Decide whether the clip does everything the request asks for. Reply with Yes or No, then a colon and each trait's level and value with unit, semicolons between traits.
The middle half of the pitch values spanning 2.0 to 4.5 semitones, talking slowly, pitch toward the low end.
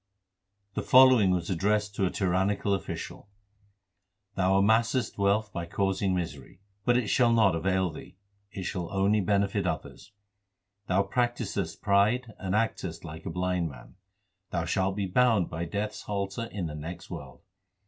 No: average, 2.8 semitones; average, 155 wpm; very low, 95 Hz